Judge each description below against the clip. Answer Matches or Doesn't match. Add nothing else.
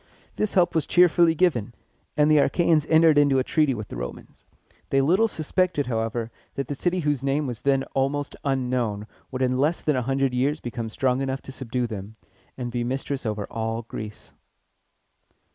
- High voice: Doesn't match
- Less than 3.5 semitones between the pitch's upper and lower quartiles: Doesn't match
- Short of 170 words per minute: Doesn't match